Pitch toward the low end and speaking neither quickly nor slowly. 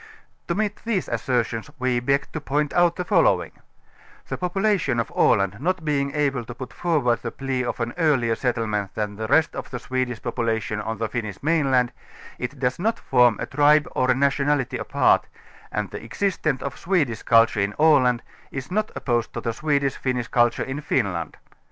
Yes: low, 130 Hz; average, 190 wpm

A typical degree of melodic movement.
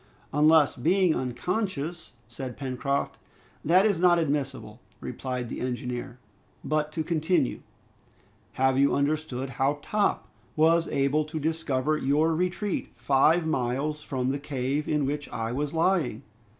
Yes: average, 3.5 semitones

